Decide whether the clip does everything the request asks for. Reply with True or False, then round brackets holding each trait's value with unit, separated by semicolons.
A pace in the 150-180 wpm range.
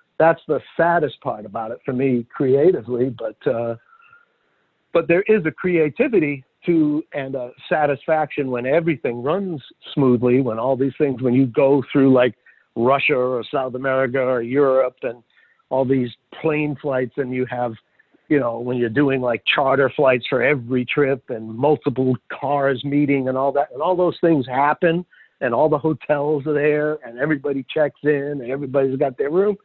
True (170 wpm)